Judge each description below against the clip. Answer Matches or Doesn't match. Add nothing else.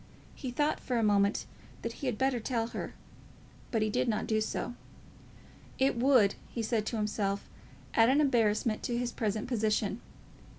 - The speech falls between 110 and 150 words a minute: Doesn't match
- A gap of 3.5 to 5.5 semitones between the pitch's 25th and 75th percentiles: Doesn't match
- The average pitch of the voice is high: Matches